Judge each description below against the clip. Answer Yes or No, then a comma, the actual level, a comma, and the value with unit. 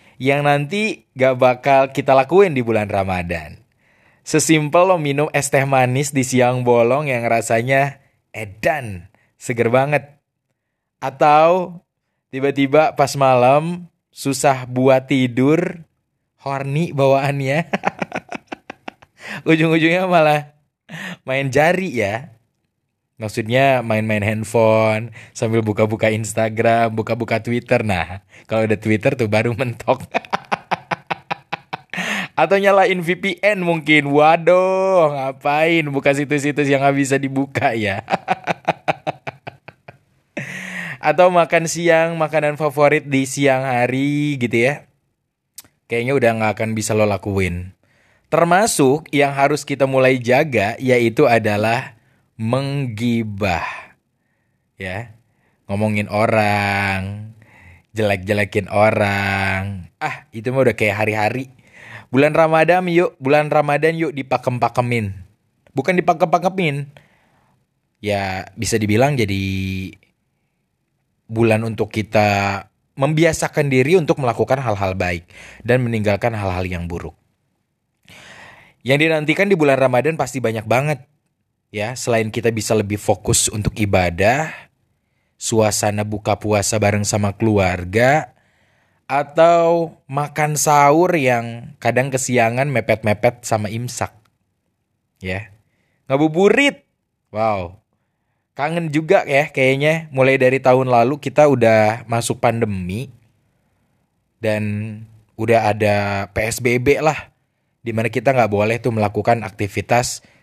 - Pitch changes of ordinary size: Yes, average, 4.9 semitones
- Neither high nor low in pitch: No, low, 125 Hz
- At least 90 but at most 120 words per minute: Yes, average, 100 wpm